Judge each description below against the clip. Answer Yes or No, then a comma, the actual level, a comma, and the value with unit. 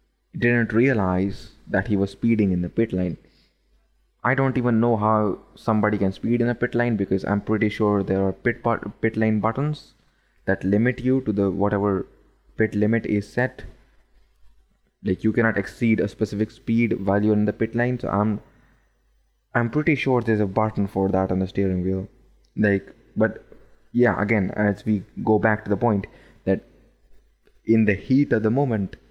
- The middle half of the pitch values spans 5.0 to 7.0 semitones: No, average, 2.8 semitones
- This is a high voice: No, low, 110 Hz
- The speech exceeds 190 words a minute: No, average, 180 wpm